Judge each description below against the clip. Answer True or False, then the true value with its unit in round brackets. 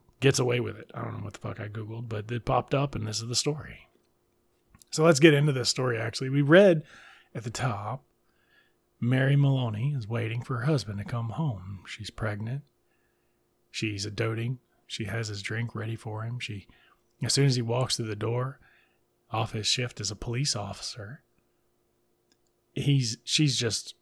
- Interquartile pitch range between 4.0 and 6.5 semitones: False (2.9 semitones)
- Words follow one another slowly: False (185 wpm)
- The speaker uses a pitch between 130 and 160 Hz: False (120 Hz)